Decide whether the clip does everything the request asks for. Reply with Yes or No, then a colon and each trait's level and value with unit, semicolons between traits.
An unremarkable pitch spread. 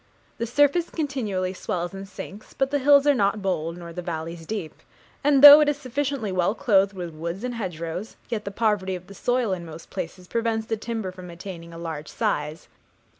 No: wide, 5.9 semitones